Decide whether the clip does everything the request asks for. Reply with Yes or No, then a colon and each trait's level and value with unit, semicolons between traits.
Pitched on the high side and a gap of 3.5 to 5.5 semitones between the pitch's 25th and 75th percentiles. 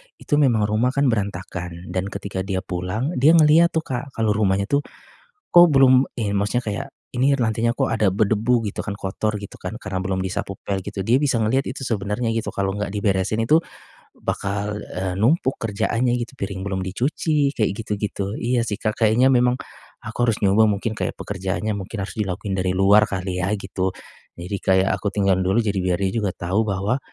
No: low, 105 Hz; average, 3.8 semitones